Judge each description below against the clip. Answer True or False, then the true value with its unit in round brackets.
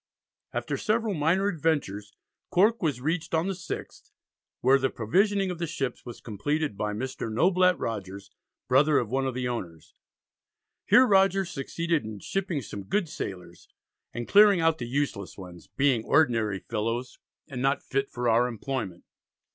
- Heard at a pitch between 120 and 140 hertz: True (135 Hz)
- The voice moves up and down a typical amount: False (7.2 semitones)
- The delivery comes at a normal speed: True (155 wpm)